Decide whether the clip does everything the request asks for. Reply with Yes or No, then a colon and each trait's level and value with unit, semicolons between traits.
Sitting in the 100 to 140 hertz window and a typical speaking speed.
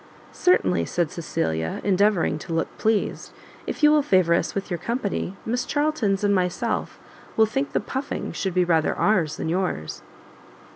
No: high, 195 Hz; average, 160 wpm